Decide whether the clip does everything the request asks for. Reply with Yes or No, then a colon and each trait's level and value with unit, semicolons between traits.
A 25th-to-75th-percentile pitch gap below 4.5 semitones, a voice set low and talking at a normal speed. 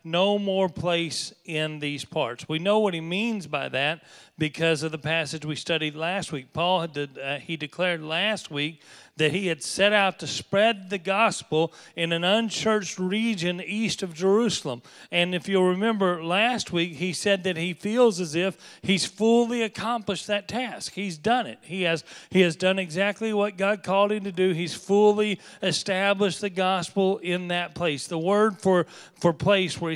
No: average, 3.6 semitones; medium, 185 Hz; average, 185 wpm